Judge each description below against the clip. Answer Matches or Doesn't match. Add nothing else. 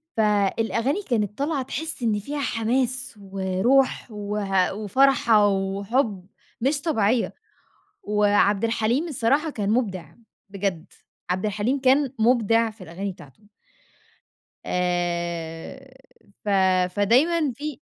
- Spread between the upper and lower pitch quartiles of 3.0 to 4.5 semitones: Doesn't match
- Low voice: Doesn't match